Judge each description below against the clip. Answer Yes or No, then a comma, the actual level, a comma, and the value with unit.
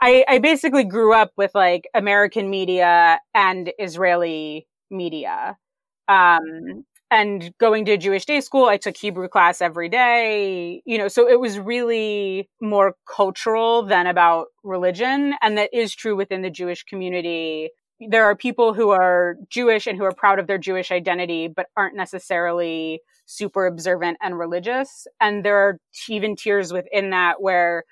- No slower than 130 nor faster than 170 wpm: Yes, average, 155 wpm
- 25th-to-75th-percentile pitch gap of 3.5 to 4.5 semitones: Yes, average, 4.1 semitones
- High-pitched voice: Yes, high, 200 Hz